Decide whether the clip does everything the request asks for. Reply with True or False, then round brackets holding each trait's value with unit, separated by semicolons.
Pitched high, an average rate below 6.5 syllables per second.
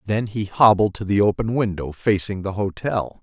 False (100 Hz; 4.9 syllables/s)